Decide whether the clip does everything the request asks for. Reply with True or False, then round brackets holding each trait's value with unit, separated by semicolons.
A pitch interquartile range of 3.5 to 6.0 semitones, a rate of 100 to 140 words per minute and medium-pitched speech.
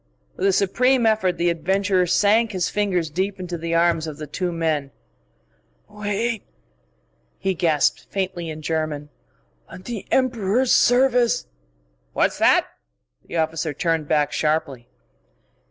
True (4.5 semitones; 135 wpm; 180 Hz)